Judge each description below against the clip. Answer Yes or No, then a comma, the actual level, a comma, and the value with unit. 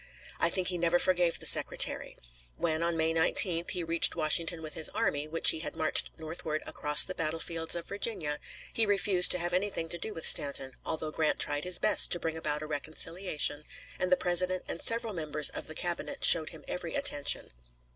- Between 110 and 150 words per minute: No, average, 195 wpm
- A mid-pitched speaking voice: Yes, medium, 165 Hz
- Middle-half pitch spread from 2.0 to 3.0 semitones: Yes, narrow, 2.4 semitones